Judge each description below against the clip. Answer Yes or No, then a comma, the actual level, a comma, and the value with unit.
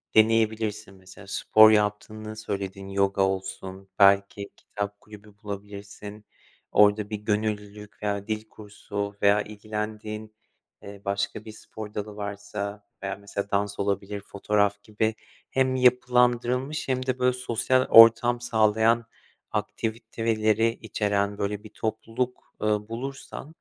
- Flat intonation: Yes, narrow, 1.6 semitones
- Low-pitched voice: Yes, low, 105 Hz